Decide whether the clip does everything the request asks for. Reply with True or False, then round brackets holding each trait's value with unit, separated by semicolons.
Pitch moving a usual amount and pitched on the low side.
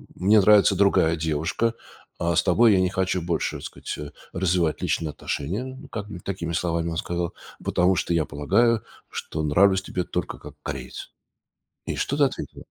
True (3.4 semitones; 90 Hz)